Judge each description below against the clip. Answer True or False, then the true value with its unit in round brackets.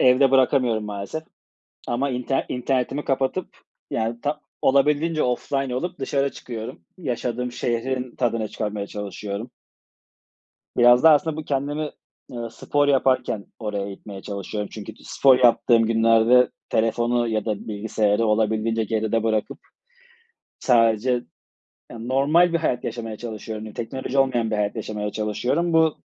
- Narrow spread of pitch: False (3.5 semitones)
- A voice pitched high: False (120 Hz)